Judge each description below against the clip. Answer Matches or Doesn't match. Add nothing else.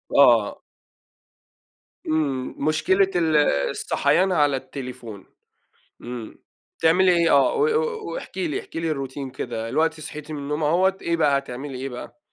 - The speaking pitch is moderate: Matches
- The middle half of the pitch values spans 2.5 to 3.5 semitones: Doesn't match